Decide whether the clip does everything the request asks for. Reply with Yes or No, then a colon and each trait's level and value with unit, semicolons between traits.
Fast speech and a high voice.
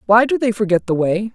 Yes: fast, 270 wpm; high, 200 Hz